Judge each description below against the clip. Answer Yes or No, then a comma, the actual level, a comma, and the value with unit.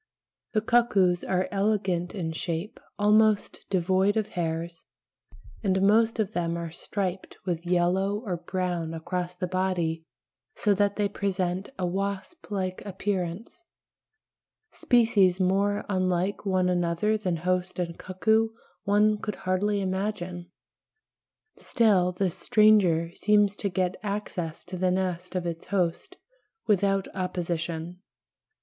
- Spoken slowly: Yes, slow, 130 wpm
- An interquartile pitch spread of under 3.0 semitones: Yes, narrow, 2.6 semitones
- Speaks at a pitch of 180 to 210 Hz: Yes, medium, 185 Hz